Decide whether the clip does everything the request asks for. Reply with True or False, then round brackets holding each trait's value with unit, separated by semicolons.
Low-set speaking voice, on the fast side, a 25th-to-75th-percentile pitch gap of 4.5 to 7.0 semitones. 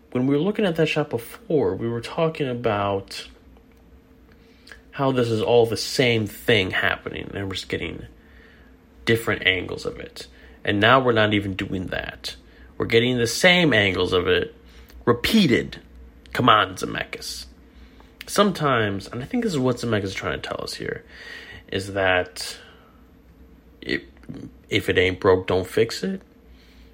False (110 Hz; 155 wpm; 5.2 semitones)